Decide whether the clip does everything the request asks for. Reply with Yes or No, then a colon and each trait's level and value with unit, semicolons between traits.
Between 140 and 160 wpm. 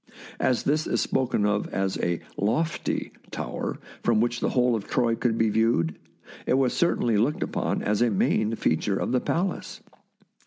No: average, 185 wpm